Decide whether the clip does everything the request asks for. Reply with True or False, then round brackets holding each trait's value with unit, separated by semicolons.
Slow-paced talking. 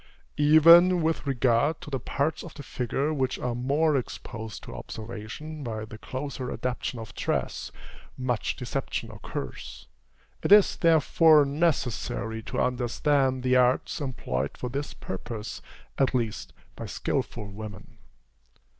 True (130 wpm)